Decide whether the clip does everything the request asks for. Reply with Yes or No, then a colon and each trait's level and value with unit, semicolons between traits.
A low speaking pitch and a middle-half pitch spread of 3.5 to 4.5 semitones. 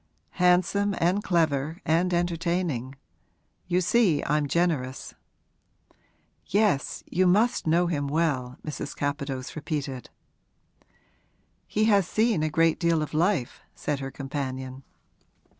No: medium, 160 Hz; average, 4.1 semitones